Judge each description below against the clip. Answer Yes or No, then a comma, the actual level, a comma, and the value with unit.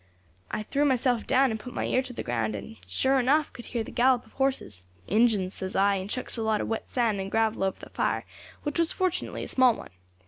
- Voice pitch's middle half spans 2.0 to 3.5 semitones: No, average, 4.7 semitones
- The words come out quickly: Yes, fast, 240 wpm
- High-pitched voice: Yes, high, 230 Hz